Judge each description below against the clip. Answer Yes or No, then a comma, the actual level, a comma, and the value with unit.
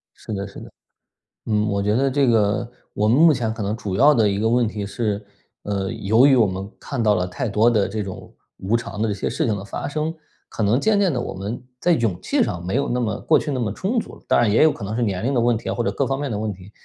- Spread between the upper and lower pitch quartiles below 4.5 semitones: Yes, average, 3.7 semitones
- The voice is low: Yes, low, 110 Hz